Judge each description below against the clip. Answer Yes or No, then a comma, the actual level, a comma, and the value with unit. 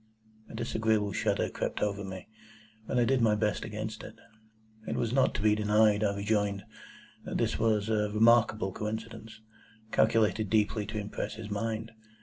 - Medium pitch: No, low, 110 Hz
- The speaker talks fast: No, average, 160 wpm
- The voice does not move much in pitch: Yes, narrow, 1.3 semitones